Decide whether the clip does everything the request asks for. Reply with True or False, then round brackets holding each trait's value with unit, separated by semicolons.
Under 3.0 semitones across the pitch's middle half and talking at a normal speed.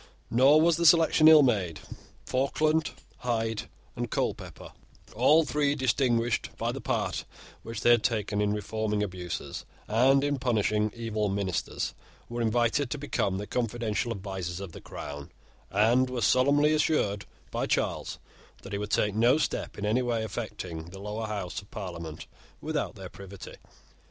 False (4.3 semitones; 155 wpm)